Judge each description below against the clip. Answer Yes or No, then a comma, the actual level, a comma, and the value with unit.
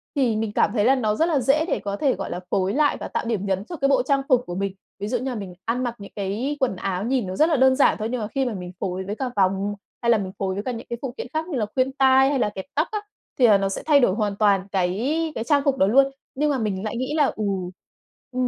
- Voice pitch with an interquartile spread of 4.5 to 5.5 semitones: Yes, average, 5.2 semitones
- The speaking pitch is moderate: No, high, 235 Hz